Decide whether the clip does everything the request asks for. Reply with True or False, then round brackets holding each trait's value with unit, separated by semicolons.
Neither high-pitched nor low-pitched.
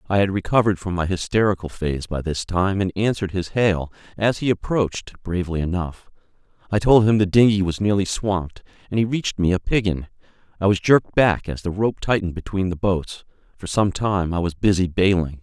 False (95 Hz)